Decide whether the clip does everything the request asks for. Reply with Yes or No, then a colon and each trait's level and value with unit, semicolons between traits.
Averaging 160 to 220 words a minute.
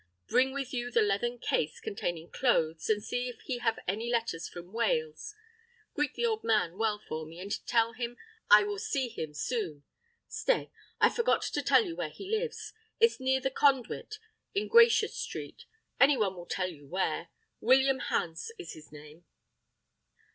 Yes: average, 175 wpm